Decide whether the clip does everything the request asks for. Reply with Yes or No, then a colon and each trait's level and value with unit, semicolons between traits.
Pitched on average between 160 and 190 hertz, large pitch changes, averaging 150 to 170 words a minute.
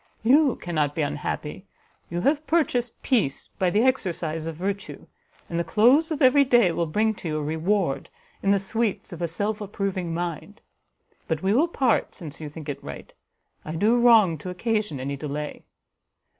No: medium, 185 Hz; wide, 6.2 semitones; average, 180 wpm